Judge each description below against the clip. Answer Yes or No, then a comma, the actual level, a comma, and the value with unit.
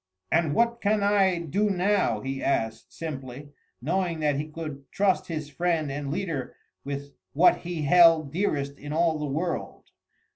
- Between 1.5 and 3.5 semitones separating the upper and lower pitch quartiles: No, average, 4.1 semitones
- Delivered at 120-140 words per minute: No, average, 155 wpm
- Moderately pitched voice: Yes, medium, 155 Hz